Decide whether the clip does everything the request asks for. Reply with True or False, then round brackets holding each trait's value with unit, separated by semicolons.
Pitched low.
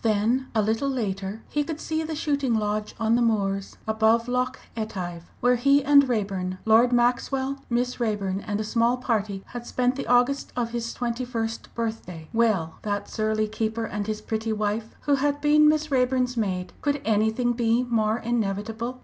False (230 Hz)